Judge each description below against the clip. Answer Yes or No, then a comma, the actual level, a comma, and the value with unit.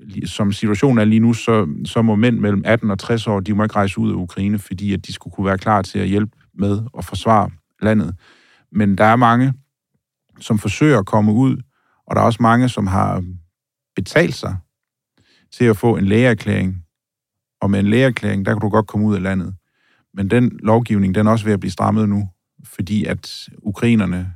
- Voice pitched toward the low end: Yes, low, 105 Hz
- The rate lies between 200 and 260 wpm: Yes, average, 205 wpm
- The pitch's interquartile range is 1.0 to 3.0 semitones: Yes, narrow, 2.5 semitones